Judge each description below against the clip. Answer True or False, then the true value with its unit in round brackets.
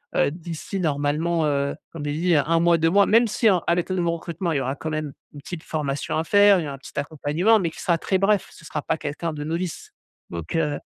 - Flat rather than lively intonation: False (3.2 semitones)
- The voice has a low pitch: False (165 Hz)